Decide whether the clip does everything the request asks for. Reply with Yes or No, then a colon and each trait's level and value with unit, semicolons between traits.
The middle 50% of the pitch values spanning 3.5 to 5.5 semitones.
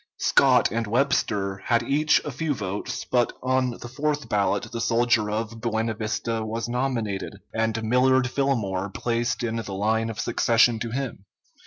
No: narrow, 2.6 semitones